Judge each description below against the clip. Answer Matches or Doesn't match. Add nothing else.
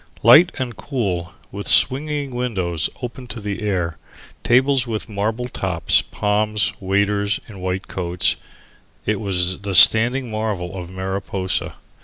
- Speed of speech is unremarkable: Doesn't match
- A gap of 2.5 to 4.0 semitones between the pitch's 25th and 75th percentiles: Doesn't match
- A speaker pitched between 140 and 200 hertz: Doesn't match